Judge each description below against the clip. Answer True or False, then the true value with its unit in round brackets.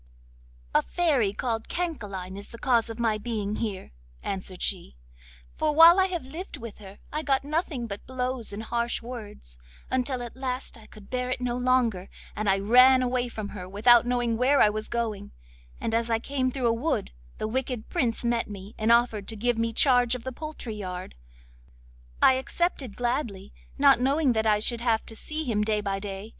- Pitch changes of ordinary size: True (3.3 semitones)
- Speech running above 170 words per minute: True (190 wpm)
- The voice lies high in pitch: True (235 Hz)